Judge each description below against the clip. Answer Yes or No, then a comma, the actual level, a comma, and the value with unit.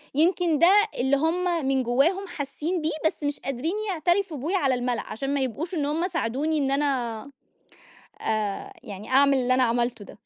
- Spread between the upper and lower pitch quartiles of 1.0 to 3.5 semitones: No, average, 4.6 semitones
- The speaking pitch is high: Yes, very high, 280 Hz